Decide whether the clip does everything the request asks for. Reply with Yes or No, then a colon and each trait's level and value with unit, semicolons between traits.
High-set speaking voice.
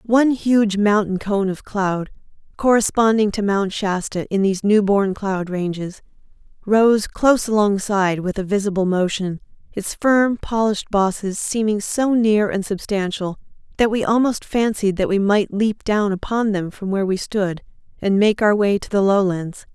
Yes: high, 205 Hz